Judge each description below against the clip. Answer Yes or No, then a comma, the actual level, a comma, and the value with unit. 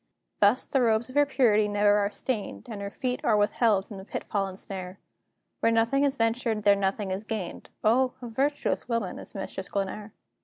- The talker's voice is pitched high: Yes, high, 215 Hz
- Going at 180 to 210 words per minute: Yes, average, 195 wpm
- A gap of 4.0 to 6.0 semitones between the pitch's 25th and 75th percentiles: No, average, 3.3 semitones